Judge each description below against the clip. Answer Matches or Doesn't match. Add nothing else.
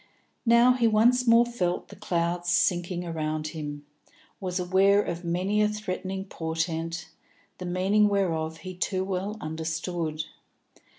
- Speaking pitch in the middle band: Matches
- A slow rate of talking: Matches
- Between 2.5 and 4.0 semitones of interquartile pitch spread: Matches